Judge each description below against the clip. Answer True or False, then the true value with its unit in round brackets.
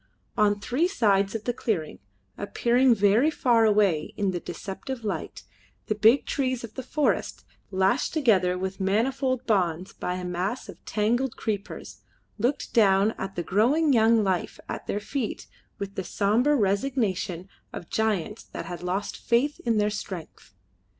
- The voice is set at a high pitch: True (210 Hz)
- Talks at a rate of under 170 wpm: True (155 wpm)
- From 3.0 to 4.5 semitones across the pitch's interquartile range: True (4.1 semitones)